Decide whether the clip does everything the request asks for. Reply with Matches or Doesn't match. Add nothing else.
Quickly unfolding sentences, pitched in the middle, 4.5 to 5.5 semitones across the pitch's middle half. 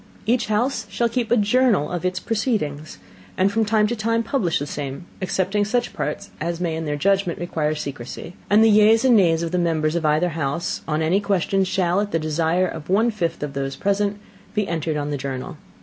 Matches